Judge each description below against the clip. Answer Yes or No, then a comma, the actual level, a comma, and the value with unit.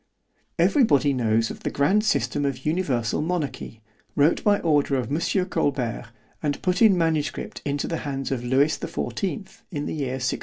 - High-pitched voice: No, medium, 145 Hz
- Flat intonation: No, average, 4.2 semitones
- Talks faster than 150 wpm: Yes, average, 180 wpm